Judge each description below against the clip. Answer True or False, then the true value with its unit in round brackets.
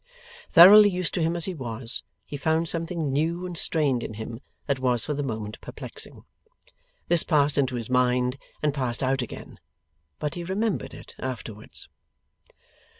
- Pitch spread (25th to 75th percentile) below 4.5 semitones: False (5.1 semitones)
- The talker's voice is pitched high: False (140 Hz)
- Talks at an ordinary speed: True (160 wpm)